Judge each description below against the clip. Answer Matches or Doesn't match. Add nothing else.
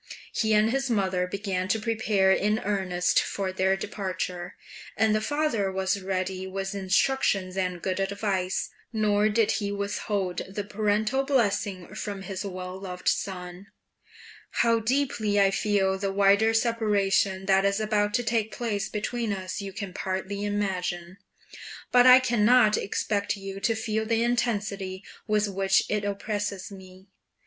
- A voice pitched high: Matches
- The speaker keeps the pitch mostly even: Matches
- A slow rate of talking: Doesn't match